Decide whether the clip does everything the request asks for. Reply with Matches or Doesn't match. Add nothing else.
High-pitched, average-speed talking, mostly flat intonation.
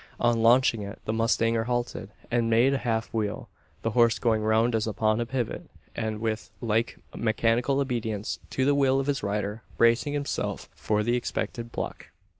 Doesn't match